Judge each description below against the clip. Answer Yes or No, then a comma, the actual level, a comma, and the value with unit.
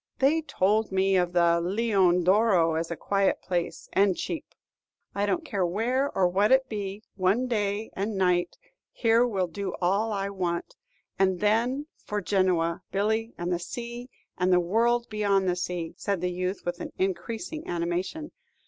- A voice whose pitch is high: Yes, high, 195 Hz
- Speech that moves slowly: No, average, 165 wpm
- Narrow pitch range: No, average, 3.8 semitones